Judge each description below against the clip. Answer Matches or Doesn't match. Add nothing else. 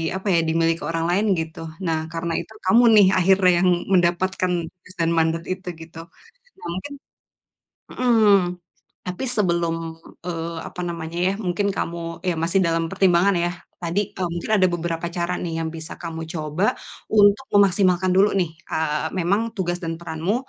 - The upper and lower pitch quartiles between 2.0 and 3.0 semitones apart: Matches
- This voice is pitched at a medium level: Matches